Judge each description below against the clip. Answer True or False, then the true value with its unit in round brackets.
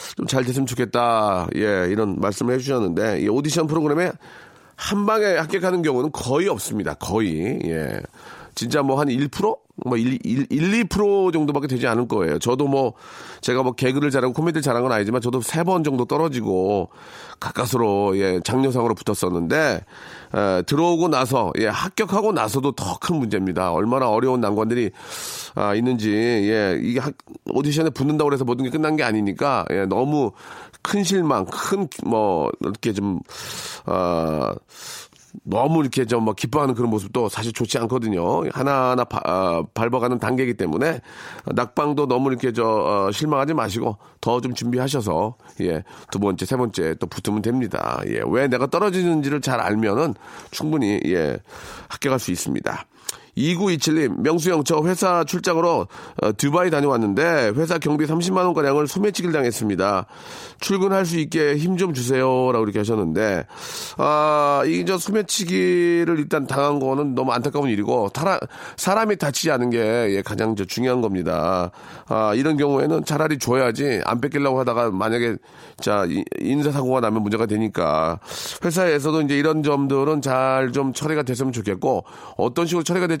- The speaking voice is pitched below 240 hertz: True (135 Hz)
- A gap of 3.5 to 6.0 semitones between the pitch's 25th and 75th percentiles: True (5.4 semitones)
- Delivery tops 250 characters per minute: True (335 characters per minute)